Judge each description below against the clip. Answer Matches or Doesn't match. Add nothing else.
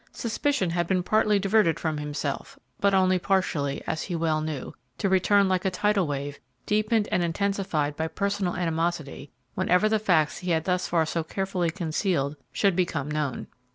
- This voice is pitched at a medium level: Matches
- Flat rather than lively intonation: Doesn't match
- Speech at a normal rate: Matches